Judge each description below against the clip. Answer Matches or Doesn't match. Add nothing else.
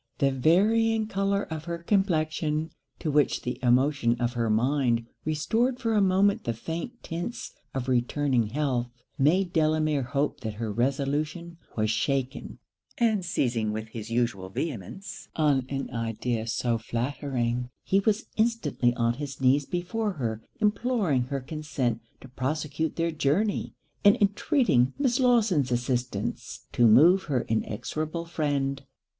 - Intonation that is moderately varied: Doesn't match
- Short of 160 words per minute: Matches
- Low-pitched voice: Doesn't match